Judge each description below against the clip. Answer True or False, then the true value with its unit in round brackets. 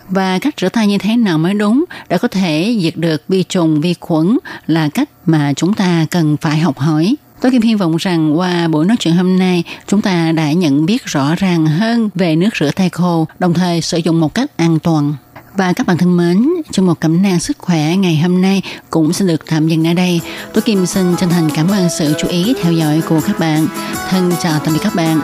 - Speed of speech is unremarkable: True (240 wpm)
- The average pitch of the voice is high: False (175 Hz)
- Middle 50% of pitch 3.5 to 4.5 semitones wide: False (3.1 semitones)